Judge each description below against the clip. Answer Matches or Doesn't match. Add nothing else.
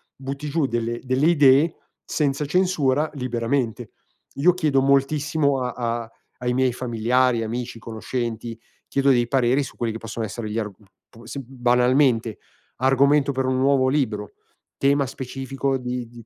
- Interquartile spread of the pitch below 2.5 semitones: Doesn't match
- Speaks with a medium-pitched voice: Doesn't match